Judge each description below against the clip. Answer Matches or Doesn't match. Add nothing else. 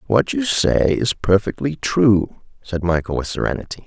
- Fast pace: Doesn't match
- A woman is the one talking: Doesn't match